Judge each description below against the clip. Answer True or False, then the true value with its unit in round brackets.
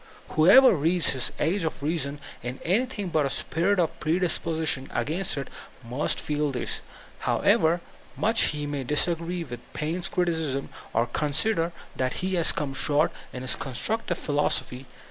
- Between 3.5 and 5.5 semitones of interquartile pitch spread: True (3.9 semitones)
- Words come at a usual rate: True (150 wpm)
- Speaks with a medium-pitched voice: True (155 Hz)